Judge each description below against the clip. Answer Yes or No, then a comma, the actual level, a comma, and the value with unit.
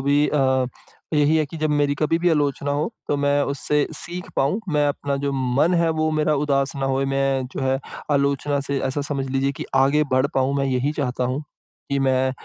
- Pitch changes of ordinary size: No, narrow, 1.6 semitones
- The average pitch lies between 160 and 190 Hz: No, medium, 140 Hz